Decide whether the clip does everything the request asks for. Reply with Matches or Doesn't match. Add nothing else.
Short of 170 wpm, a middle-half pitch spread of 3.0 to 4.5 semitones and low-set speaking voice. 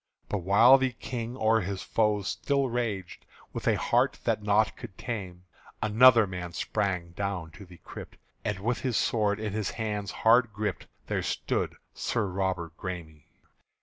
Matches